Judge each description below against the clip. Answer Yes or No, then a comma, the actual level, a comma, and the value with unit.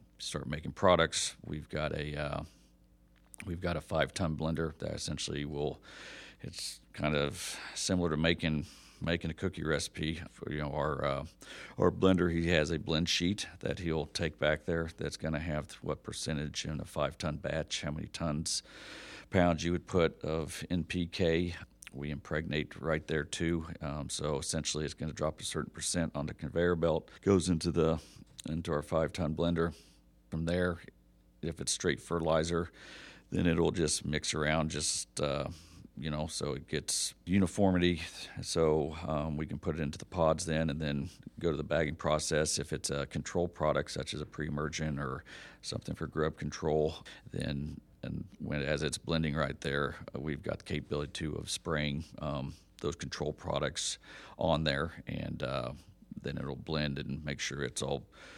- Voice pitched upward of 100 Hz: No, very low, 80 Hz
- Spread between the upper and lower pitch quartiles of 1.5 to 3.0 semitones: Yes, narrow, 2.5 semitones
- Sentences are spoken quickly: No, average, 175 wpm